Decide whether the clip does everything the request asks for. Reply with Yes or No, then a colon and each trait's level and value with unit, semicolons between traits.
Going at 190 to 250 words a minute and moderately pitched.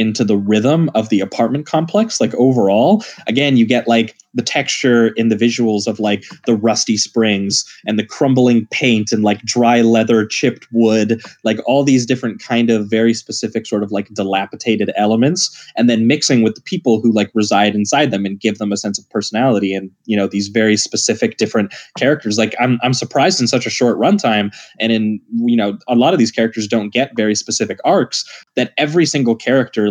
No: average, 200 wpm; low, 115 Hz